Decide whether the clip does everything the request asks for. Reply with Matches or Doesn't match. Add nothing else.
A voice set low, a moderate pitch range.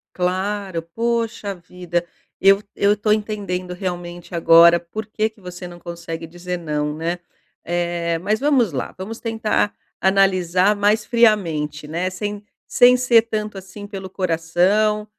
Doesn't match